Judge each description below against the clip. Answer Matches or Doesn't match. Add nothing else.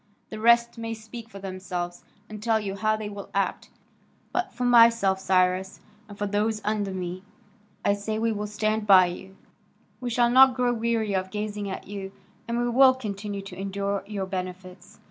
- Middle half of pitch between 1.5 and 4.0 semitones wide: Matches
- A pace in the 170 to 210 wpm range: Matches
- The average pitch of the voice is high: Matches